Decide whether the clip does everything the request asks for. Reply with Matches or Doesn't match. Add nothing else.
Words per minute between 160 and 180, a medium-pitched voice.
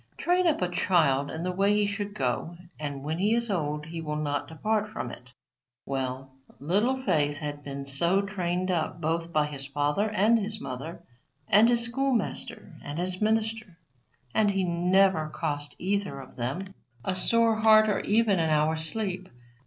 Matches